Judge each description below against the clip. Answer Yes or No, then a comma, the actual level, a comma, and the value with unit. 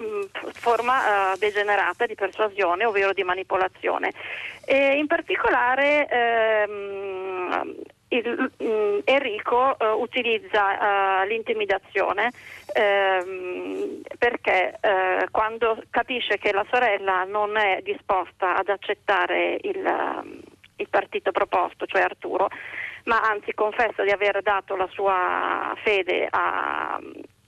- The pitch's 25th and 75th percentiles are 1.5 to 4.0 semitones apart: No, average, 4.5 semitones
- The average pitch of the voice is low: No, high, 215 Hz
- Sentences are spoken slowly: Yes, slow, 105 wpm